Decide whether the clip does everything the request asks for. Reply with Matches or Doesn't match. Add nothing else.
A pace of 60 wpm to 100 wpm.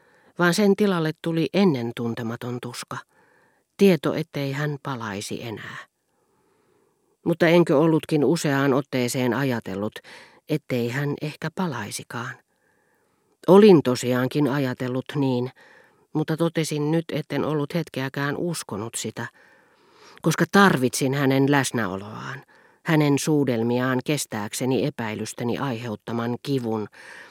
Matches